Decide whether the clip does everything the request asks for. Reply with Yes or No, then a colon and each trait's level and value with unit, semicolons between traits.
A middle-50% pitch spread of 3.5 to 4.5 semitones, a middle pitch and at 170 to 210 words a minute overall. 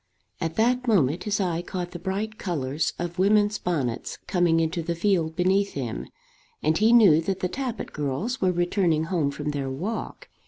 Yes: average, 4.2 semitones; medium, 175 Hz; average, 180 wpm